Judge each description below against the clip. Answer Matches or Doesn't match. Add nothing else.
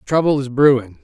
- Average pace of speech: Matches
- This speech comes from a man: Matches